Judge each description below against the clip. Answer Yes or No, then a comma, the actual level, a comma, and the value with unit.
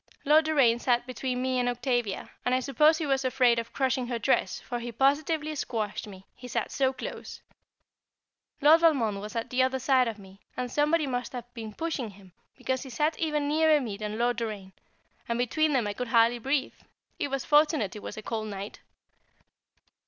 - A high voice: Yes, very high, 250 Hz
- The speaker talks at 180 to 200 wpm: Yes, average, 195 wpm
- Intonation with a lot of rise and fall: No, average, 3.7 semitones